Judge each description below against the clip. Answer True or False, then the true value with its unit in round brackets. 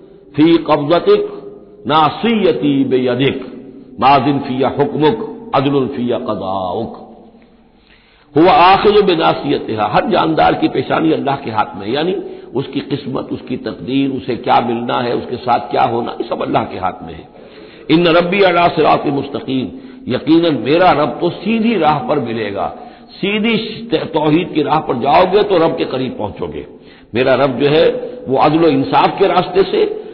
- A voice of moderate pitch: True (175 Hz)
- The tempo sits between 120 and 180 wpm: True (155 wpm)